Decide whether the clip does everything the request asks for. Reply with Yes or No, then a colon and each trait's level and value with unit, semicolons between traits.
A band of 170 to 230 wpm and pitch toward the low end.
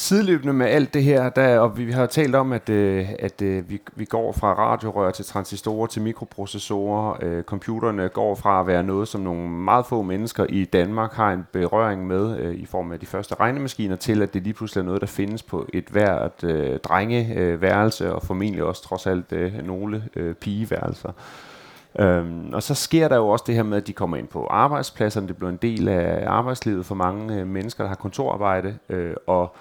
Yes: average, 210 wpm; low, 100 Hz